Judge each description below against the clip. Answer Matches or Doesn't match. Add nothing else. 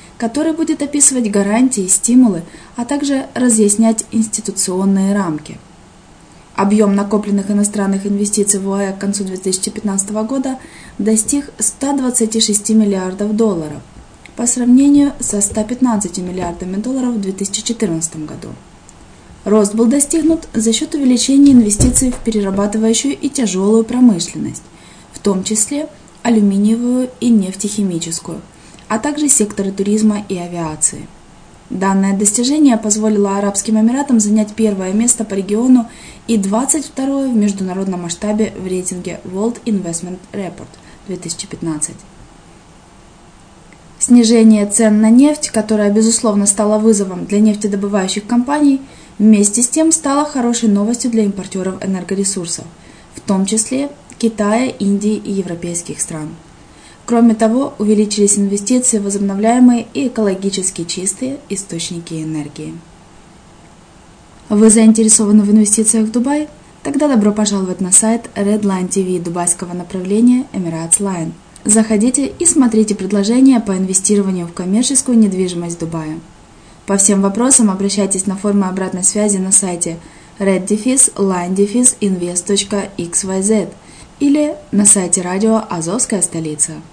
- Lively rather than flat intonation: Doesn't match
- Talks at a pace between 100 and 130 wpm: Matches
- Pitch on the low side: Doesn't match